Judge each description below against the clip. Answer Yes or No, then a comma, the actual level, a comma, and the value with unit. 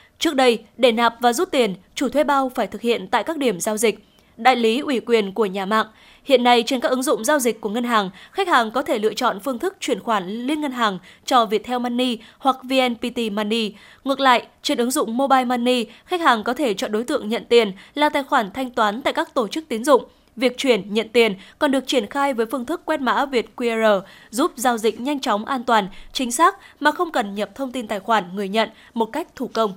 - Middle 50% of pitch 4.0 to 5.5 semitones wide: No, average, 3.6 semitones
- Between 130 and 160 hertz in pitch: No, high, 245 Hz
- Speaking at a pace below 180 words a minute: No, average, 240 wpm